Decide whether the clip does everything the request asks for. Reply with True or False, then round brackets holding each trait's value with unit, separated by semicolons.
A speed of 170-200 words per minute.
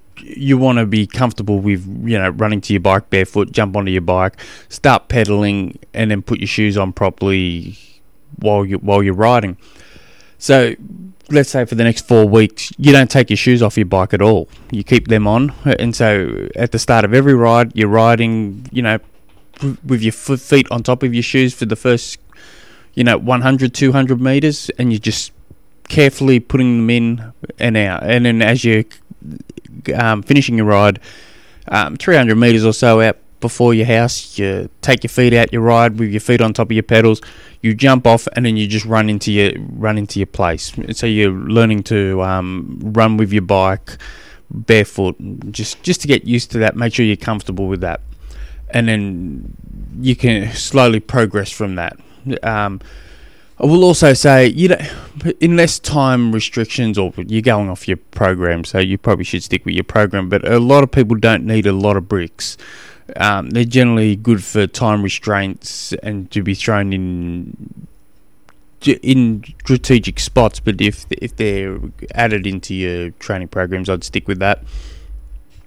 True (185 wpm)